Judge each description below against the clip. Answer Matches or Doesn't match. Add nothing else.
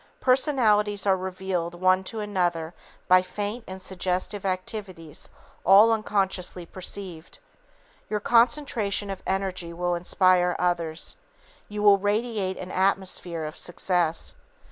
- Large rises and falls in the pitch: Doesn't match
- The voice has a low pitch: Doesn't match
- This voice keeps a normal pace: Doesn't match